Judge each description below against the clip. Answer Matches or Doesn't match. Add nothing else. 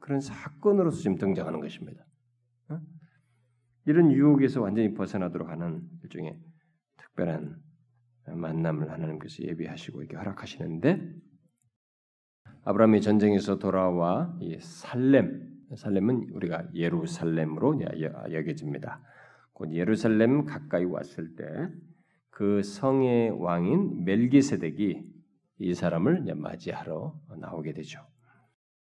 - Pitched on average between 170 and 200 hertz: Doesn't match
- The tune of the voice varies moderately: Doesn't match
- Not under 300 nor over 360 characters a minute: Doesn't match